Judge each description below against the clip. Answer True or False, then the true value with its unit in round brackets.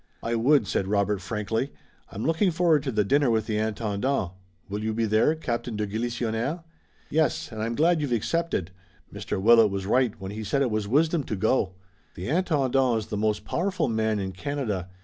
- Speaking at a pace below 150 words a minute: False (190 wpm)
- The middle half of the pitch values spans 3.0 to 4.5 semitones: False (5.0 semitones)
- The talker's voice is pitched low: True (115 Hz)